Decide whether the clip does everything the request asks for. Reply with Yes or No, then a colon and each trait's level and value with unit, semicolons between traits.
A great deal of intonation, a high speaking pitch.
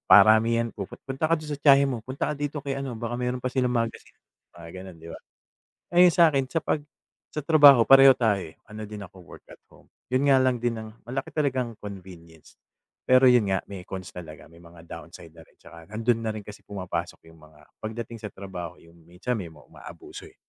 No: wide, 6.1 semitones; low, 115 Hz